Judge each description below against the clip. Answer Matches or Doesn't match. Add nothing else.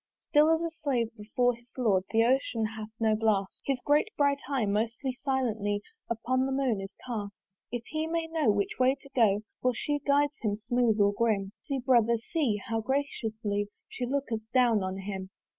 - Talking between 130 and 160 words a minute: Doesn't match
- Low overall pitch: Doesn't match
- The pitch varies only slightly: Doesn't match